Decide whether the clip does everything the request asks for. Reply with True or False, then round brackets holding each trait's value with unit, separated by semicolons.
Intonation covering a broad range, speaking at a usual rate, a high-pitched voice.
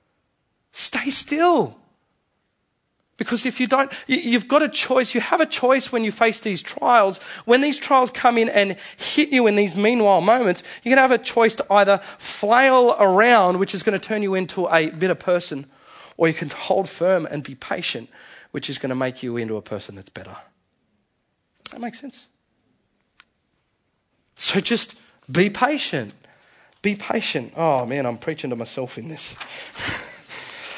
True (6.2 semitones; 165 wpm; 215 Hz)